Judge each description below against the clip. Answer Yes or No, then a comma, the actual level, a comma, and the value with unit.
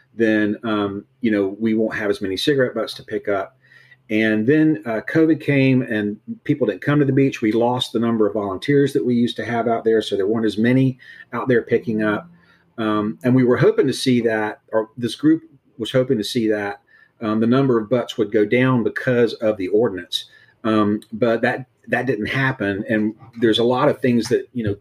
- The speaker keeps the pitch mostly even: No, average, 3.3 semitones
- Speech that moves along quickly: Yes, fast, 220 wpm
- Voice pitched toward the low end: Yes, low, 115 Hz